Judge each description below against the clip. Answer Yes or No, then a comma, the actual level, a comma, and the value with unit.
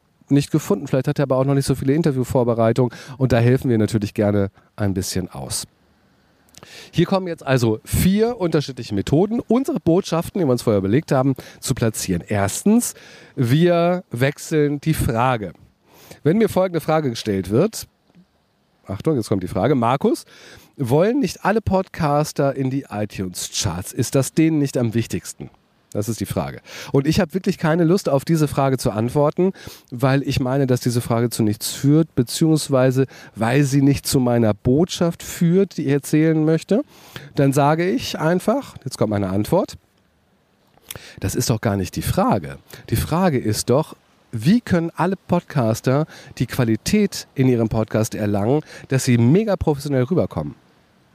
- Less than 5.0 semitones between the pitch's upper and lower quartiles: No, wide, 5.6 semitones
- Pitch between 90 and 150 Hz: Yes, low, 135 Hz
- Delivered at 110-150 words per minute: No, average, 160 wpm